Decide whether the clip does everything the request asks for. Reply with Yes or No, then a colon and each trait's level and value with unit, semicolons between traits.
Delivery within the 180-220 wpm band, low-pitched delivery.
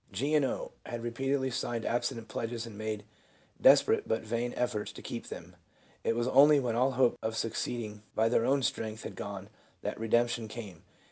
Yes: average, 195 wpm; low, 115 Hz